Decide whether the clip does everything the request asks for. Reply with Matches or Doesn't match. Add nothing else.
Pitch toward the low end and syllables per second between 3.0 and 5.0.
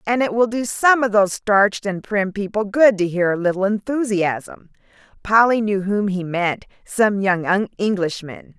Doesn't match